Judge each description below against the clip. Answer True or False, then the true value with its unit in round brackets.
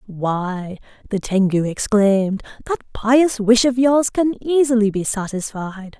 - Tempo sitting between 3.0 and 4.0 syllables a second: True (3.9 syllables/s)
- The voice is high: True (220 Hz)